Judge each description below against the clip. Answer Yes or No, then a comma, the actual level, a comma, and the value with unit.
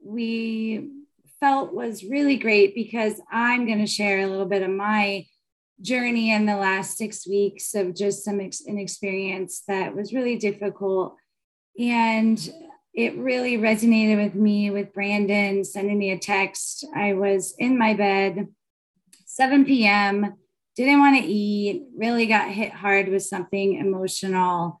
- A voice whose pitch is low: No, high, 205 Hz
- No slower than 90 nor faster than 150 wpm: Yes, average, 145 wpm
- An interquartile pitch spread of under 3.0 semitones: Yes, narrow, 2.6 semitones